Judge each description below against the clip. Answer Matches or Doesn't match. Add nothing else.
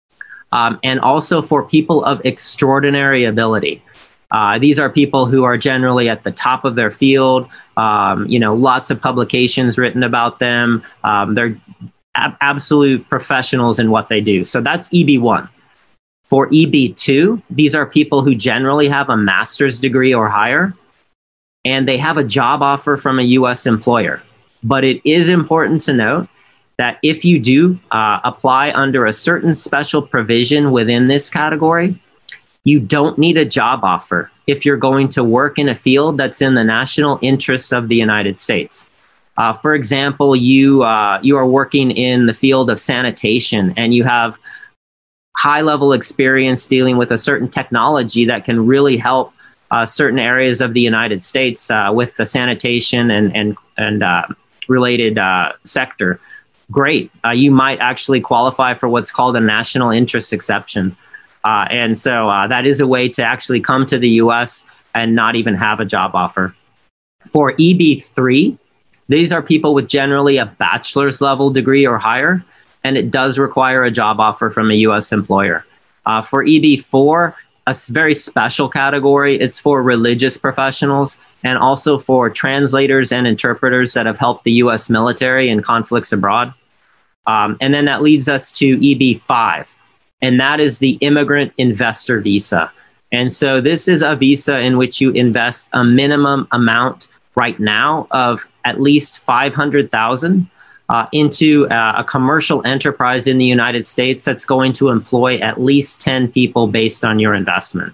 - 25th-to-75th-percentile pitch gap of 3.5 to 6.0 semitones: Doesn't match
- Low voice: Matches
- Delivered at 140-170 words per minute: Matches